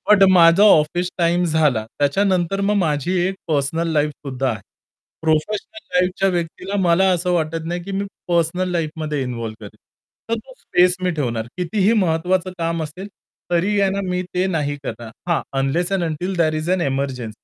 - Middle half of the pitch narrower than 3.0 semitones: No, average, 3.6 semitones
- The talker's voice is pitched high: No, medium, 170 Hz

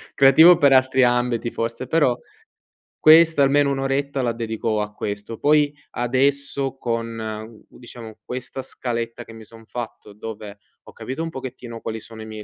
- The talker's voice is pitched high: No, low, 120 Hz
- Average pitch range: Yes, average, 3.3 semitones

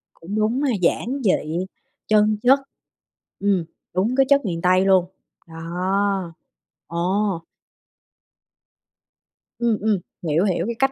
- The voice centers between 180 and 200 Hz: Yes, high, 195 Hz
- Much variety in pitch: No, average, 3.8 semitones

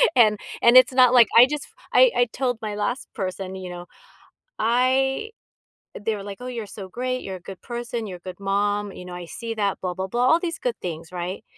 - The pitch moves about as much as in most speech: Yes, average, 4.8 semitones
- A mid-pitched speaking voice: No, high, 215 Hz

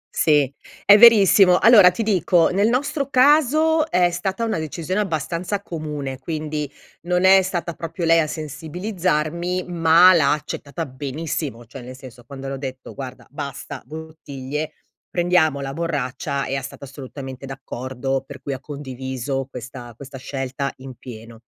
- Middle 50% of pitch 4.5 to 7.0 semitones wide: Yes, average, 5.0 semitones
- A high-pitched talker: No, medium, 150 Hz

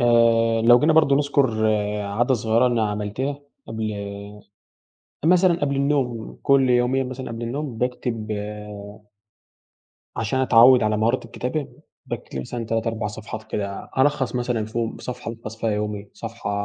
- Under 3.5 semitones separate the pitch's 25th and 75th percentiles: Yes, average, 3.1 semitones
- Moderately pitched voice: No, low, 115 Hz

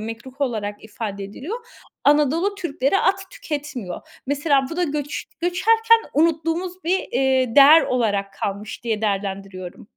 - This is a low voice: No, very high, 275 Hz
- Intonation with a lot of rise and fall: Yes, wide, 7.8 semitones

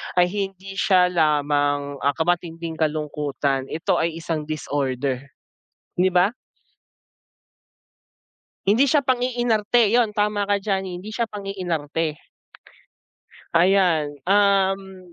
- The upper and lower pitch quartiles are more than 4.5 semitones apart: Yes, average, 4.9 semitones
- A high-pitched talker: No, medium, 180 Hz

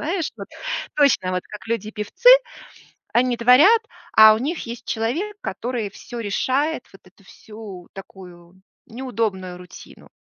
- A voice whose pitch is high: Yes, high, 225 Hz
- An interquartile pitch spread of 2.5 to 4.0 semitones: No, average, 5.1 semitones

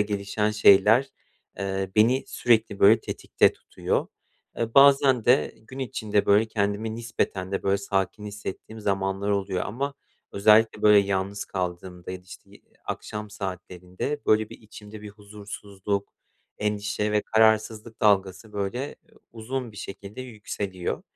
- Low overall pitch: Yes, low, 105 Hz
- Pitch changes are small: Yes, narrow, 2.1 semitones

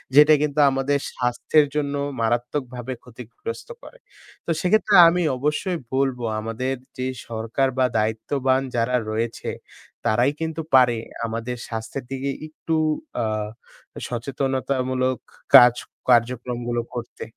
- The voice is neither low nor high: No, low, 125 Hz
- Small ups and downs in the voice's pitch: No, average, 3.1 semitones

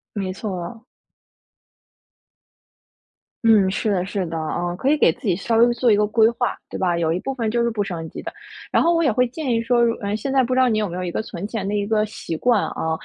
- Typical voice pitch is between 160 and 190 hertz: No, high, 215 Hz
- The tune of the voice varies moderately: Yes, average, 4.4 semitones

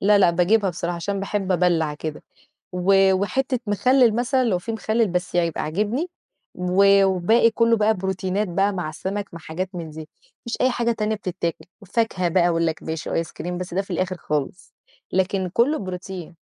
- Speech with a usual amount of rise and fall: Yes, average, 3.3 semitones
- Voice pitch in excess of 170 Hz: Yes, high, 190 Hz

